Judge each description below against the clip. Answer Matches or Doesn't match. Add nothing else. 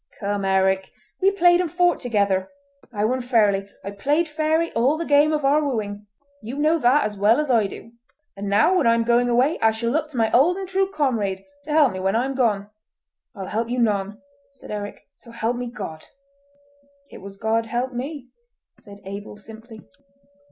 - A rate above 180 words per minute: Matches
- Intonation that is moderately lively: Doesn't match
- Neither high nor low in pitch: Doesn't match